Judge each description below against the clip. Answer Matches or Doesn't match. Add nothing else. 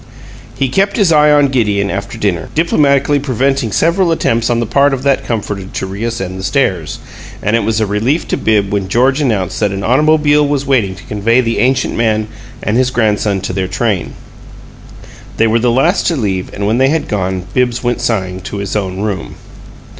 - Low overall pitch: Matches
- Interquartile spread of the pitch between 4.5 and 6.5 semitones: Matches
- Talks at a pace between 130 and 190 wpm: Doesn't match